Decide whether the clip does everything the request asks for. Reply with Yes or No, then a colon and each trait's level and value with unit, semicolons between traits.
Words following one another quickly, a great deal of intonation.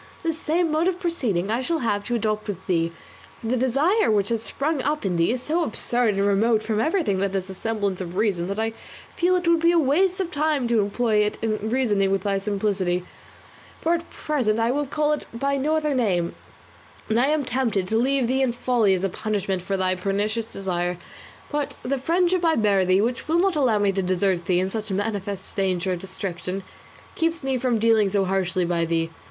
Yes: fast, 225 wpm; wide, 6.2 semitones